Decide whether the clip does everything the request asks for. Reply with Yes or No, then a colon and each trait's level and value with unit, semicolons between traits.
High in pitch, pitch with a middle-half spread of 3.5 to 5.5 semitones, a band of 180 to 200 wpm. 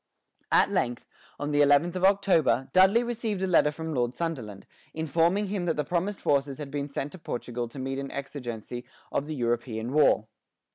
No: medium, 145 Hz; average, 5.2 semitones; average, 185 wpm